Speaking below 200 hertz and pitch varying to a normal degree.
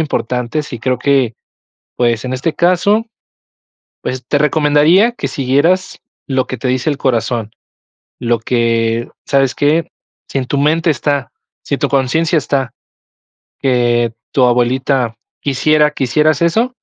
Yes: low, 135 Hz; average, 3.7 semitones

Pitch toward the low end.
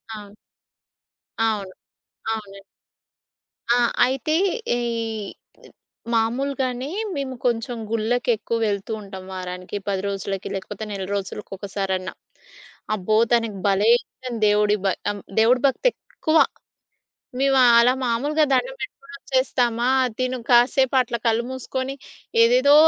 No: high, 230 Hz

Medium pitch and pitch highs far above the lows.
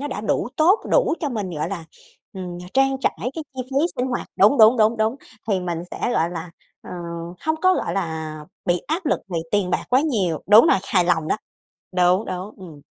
No: high, 205 Hz; wide, 6.8 semitones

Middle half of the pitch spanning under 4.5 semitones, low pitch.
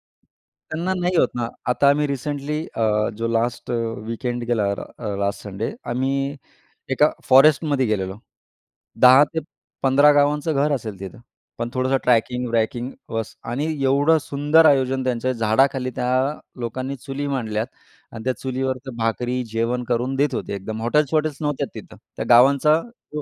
Yes: average, 3.6 semitones; low, 130 Hz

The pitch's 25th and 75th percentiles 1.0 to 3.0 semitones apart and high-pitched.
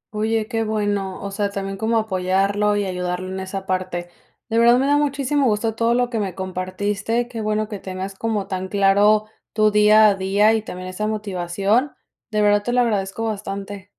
Yes: narrow, 2.5 semitones; high, 205 Hz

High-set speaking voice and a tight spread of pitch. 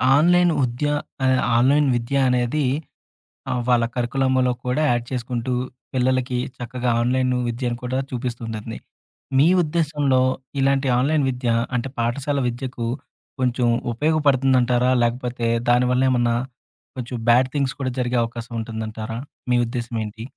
No: low, 125 Hz; narrow, 1.9 semitones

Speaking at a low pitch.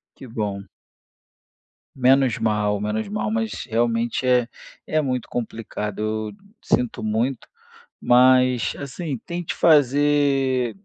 Yes: low, 120 Hz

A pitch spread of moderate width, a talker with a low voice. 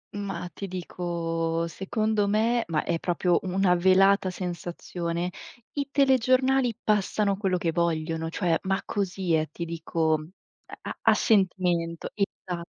No: average, 3.2 semitones; medium, 180 Hz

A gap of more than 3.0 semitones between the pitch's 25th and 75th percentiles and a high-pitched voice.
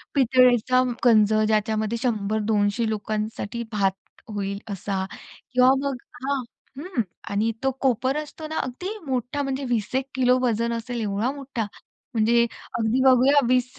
Yes: average, 3.4 semitones; high, 235 Hz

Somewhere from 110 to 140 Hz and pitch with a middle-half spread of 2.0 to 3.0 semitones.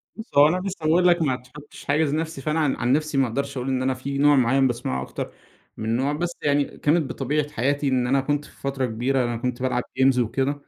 Yes: low, 135 Hz; average, 2.7 semitones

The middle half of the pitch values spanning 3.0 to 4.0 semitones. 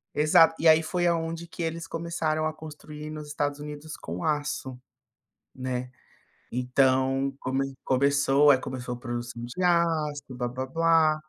Yes: average, 3.5 semitones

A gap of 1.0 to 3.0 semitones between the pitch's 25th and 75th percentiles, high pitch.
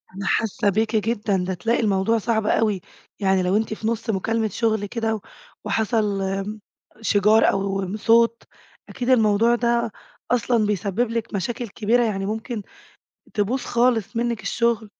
Yes: narrow, 2.4 semitones; high, 220 Hz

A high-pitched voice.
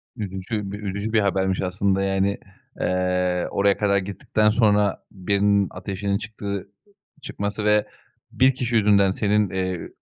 No: low, 100 Hz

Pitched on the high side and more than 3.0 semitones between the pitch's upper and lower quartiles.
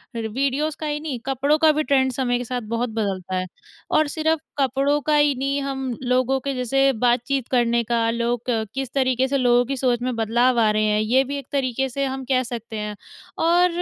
No: very high, 255 Hz; average, 2.7 semitones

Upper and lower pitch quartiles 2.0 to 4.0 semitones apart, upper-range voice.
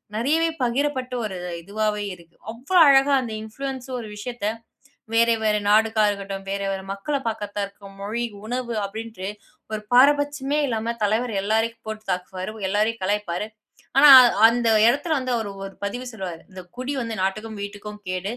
Yes: average, 3.6 semitones; high, 220 Hz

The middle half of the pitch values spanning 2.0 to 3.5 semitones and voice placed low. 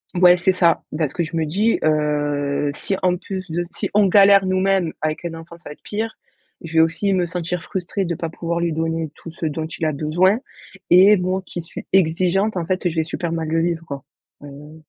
No: average, 2.8 semitones; medium, 170 Hz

